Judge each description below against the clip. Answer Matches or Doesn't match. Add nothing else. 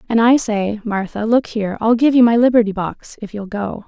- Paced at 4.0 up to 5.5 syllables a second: Matches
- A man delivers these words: Doesn't match